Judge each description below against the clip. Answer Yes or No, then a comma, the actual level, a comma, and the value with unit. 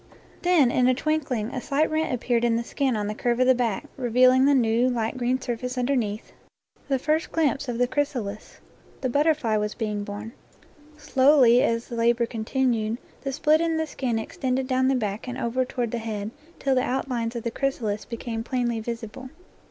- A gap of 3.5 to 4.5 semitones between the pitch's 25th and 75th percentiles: No, average, 2.7 semitones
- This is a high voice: Yes, high, 245 Hz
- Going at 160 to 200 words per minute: Yes, average, 190 wpm